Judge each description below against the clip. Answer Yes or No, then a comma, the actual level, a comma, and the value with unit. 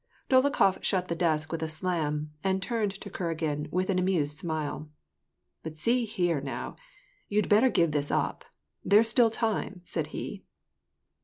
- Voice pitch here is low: No, medium, 180 Hz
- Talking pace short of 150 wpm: No, average, 165 wpm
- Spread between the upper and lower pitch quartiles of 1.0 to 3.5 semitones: No, average, 4.8 semitones